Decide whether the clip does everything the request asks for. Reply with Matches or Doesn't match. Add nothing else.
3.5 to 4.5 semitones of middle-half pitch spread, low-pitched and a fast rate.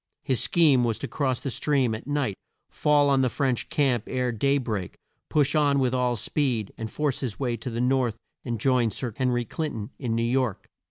Doesn't match